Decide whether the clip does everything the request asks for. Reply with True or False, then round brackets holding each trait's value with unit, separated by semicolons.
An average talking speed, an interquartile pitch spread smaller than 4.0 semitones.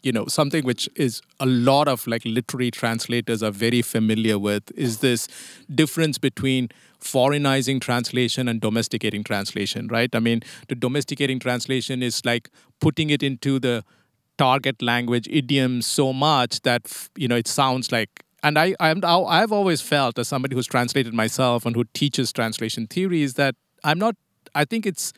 True (165 wpm; 3.3 semitones)